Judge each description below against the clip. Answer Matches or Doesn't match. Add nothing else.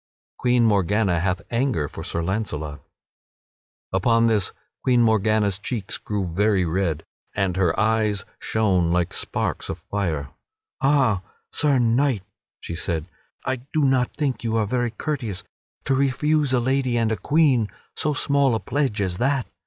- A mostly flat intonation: Doesn't match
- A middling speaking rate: Matches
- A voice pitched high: Doesn't match